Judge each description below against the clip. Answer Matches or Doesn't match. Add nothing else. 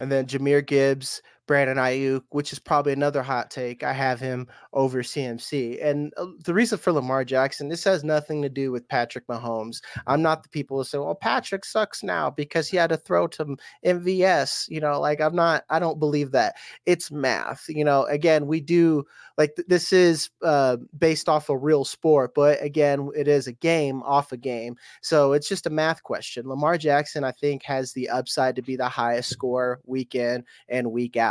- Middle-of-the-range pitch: Matches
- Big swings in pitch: Doesn't match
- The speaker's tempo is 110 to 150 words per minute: Doesn't match